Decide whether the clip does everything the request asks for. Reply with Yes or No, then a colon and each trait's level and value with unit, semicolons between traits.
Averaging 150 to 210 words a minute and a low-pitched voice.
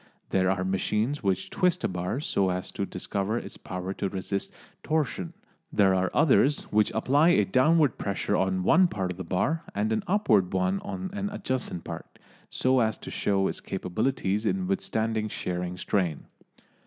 Yes: average, 170 wpm; low, 100 Hz